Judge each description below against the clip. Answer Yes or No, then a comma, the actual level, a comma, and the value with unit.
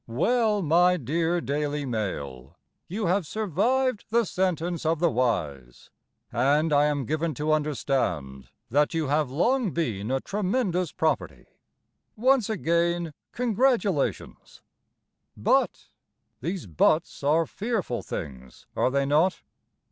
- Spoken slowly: Yes, slow, 115 wpm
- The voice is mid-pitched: Yes, medium, 160 Hz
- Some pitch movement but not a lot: No, wide, 6.0 semitones